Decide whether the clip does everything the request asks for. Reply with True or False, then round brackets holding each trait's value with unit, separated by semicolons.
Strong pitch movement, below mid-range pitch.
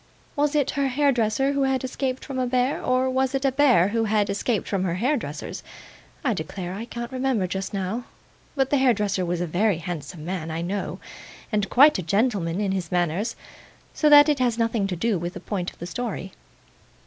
False (6.0 semitones; 220 Hz)